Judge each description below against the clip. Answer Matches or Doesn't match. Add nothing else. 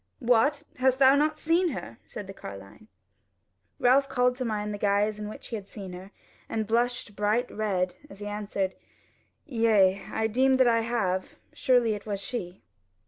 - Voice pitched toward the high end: Matches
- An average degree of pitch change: Matches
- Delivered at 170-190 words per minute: Matches